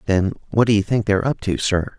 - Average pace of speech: No, fast, 270 wpm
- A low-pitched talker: Yes, low, 100 Hz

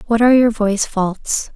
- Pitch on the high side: Yes, high, 220 Hz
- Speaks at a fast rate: No, average, 195 wpm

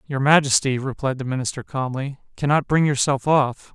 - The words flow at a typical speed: Yes, average, 160 wpm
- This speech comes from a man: Yes, male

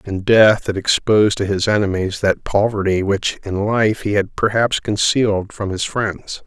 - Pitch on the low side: Yes, low, 105 Hz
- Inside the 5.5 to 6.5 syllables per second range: No, 4.5 syllables/s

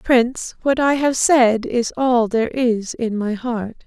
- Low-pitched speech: No, high, 245 Hz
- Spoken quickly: No, average, 185 wpm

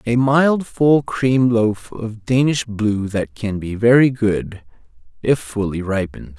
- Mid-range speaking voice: No, low, 115 Hz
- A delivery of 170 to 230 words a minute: No, average, 150 wpm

